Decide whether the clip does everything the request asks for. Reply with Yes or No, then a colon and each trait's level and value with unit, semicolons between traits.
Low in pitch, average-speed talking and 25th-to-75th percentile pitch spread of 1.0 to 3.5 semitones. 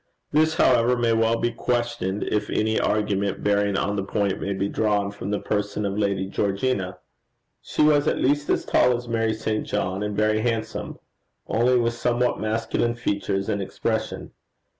Yes: low, 110 Hz; average, 170 wpm; average, 2.8 semitones